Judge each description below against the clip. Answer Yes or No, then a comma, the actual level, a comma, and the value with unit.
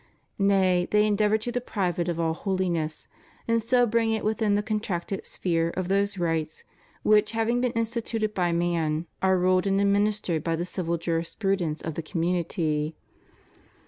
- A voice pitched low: No, high, 190 Hz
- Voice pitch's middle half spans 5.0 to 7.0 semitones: No, average, 4.0 semitones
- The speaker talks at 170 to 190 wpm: No, average, 160 wpm